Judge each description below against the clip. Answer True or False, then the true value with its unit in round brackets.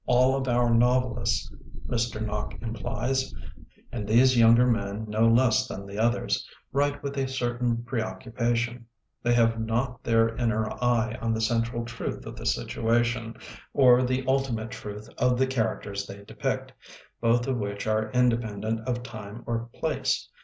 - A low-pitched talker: True (120 Hz)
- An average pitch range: False (1.9 semitones)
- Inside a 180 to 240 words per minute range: False (160 wpm)